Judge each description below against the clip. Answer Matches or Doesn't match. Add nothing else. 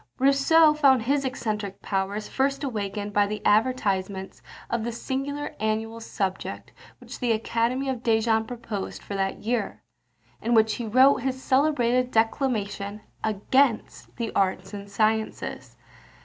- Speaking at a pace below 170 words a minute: Matches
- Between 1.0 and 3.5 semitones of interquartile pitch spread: Doesn't match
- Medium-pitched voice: Doesn't match